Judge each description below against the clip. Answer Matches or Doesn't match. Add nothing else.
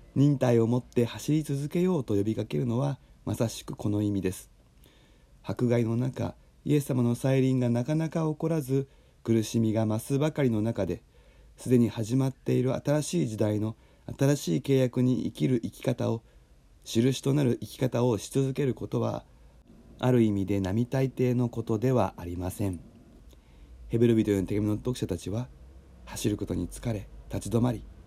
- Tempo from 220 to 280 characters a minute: Doesn't match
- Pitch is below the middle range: Matches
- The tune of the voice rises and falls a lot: Doesn't match